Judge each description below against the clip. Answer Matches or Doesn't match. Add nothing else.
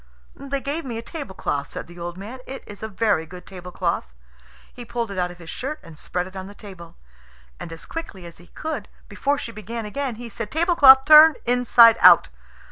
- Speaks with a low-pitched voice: Doesn't match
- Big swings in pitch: Matches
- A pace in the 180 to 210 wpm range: Matches